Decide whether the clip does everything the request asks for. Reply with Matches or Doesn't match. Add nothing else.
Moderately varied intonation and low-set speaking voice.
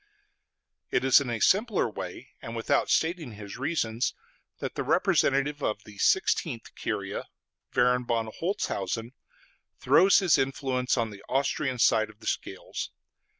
Matches